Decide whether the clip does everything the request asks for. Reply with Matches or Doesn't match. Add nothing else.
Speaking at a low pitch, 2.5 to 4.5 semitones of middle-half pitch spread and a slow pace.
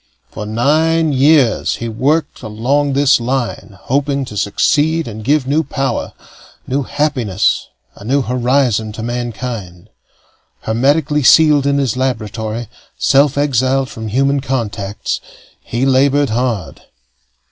Matches